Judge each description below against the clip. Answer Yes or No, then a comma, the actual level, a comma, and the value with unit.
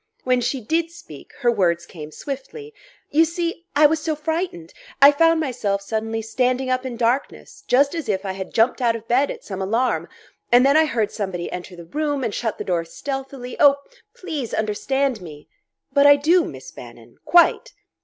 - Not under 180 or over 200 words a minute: Yes, average, 185 wpm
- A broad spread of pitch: Yes, wide, 5.9 semitones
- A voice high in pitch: Yes, very high, 255 Hz